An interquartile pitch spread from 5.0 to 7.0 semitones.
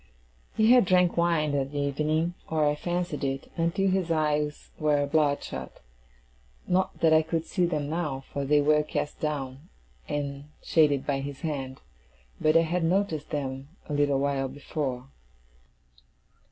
No: average, 2.7 semitones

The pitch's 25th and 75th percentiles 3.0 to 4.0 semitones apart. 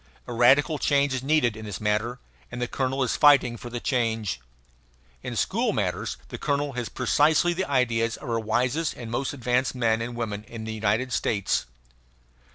Yes: average, 3.3 semitones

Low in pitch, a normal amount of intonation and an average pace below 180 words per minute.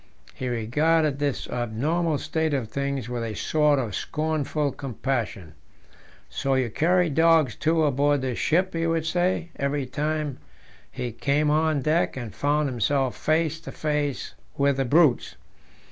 No: medium, 145 Hz; average, 3.4 semitones; average, 145 wpm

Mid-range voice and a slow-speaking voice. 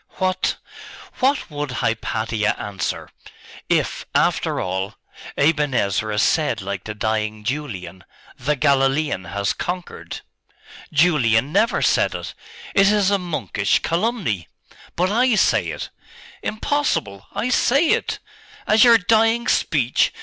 Yes: medium, 145 Hz; slow, 120 wpm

